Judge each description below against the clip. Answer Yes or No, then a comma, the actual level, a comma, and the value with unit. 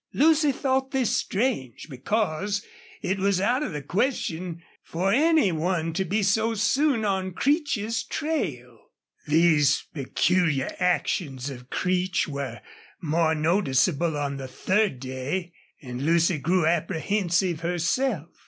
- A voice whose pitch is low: No, medium, 180 Hz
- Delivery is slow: Yes, slow, 125 wpm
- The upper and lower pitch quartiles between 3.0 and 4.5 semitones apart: No, wide, 5.6 semitones